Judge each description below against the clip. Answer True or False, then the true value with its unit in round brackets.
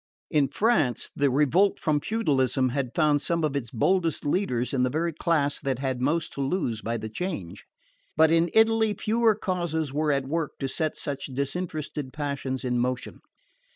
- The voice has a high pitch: False (145 Hz)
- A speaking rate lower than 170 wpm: False (175 wpm)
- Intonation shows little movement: False (4.3 semitones)